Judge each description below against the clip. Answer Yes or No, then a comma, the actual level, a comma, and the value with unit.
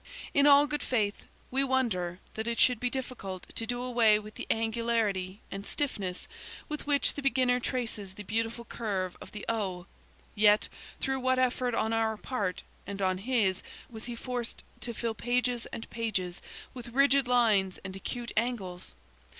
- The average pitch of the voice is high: Yes, high, 230 Hz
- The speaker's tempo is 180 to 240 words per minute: No, average, 170 wpm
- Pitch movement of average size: Yes, average, 3.6 semitones